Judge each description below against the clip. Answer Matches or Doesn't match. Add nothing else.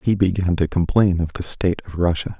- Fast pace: Matches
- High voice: Doesn't match